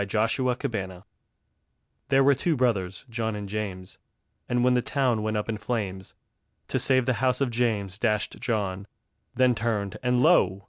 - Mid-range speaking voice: No, low, 115 Hz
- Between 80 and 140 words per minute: No, average, 170 wpm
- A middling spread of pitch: Yes, average, 3.7 semitones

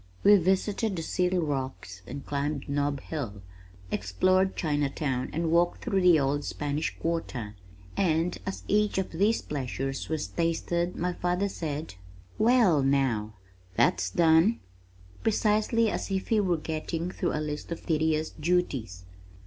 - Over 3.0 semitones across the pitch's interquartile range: Yes, average, 4.5 semitones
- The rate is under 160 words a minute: Yes, average, 140 wpm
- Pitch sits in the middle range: Yes, medium, 160 Hz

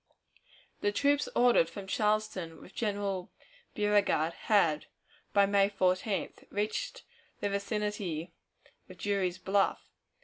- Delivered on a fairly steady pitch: Yes, narrow, 2.1 semitones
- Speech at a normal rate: No, slow, 105 wpm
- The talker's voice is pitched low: No, high, 200 Hz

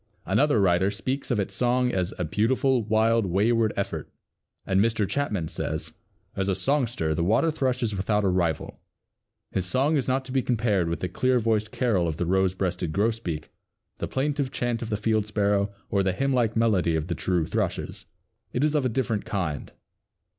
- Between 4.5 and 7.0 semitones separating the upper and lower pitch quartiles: Yes, average, 4.9 semitones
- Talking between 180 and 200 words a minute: Yes, average, 190 wpm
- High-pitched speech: No, low, 105 Hz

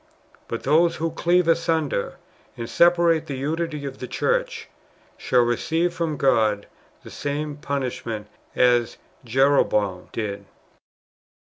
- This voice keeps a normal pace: No, slow, 115 wpm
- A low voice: No, medium, 145 Hz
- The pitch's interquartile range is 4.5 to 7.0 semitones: Yes, wide, 5.6 semitones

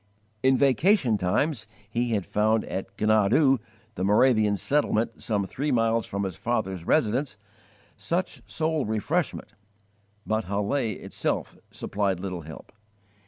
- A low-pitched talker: Yes, low, 110 Hz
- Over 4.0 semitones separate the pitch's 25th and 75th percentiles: Yes, average, 4.9 semitones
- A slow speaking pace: Yes, slow, 120 wpm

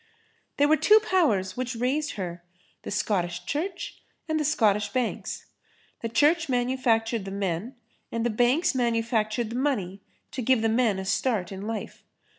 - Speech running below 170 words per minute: Yes, average, 155 wpm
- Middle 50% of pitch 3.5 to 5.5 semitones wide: Yes, average, 4.6 semitones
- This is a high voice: Yes, high, 230 Hz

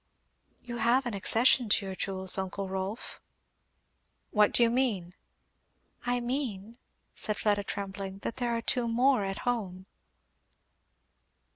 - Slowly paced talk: Yes, slow, 130 wpm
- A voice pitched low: No, high, 215 Hz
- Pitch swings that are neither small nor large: Yes, average, 3.8 semitones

